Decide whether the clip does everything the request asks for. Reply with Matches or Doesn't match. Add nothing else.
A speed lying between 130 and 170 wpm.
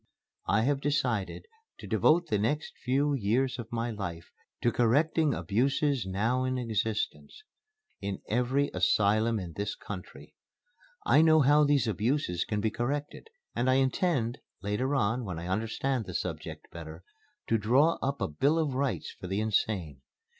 Matches